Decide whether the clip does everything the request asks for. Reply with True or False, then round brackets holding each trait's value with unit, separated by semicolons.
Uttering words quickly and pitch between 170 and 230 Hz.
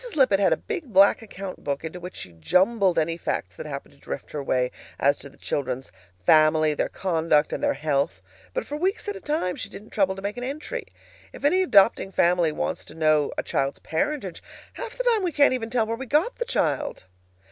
True (220 wpm; 190 Hz)